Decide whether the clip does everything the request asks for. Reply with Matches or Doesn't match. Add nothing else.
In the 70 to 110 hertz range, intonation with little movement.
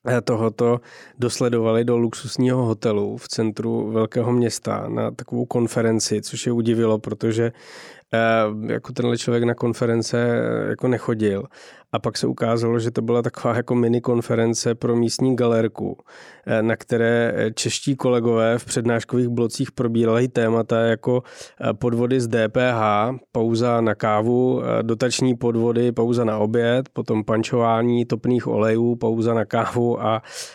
Doesn't match